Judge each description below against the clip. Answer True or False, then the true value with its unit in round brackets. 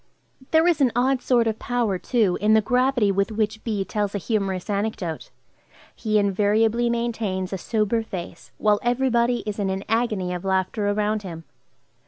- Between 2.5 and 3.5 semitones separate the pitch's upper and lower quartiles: True (3.1 semitones)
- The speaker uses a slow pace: False (175 wpm)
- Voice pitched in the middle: False (215 Hz)